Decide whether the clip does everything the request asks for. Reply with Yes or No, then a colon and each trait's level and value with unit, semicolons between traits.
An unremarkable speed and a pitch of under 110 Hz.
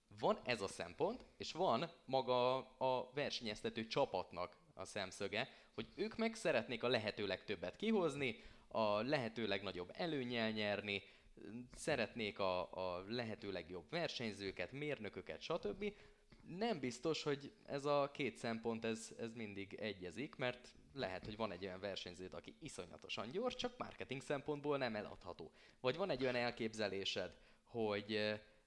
No: average, 135 wpm; low, 115 Hz